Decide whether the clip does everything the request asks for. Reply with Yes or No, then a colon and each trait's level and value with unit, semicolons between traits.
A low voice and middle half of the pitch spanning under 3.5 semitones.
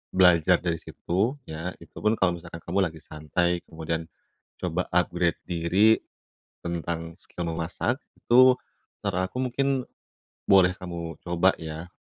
Yes: very low, 90 Hz; average, 2.9 semitones